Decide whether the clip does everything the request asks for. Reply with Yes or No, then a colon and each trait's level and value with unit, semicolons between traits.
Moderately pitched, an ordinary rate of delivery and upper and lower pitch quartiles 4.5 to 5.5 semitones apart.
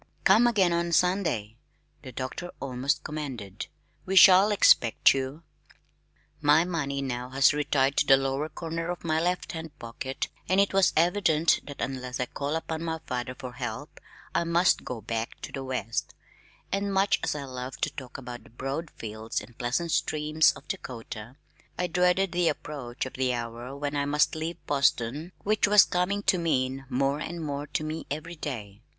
Yes: medium, 145 Hz; average, 180 wpm; average, 4.9 semitones